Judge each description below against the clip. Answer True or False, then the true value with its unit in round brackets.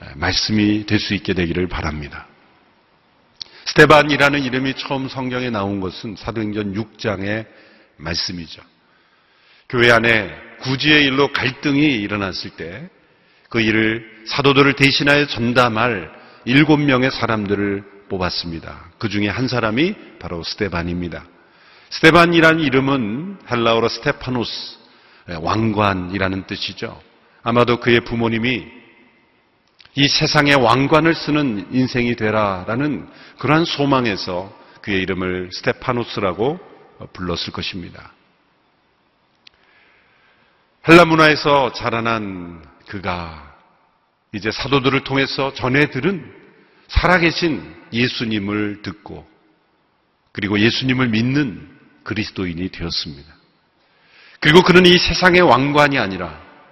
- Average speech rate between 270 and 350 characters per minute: False (260 characters per minute)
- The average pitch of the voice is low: True (115 Hz)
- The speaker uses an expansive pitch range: True (5.8 semitones)